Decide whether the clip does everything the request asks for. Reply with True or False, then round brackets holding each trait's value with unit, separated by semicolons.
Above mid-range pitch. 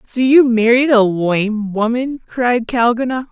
True (235 Hz)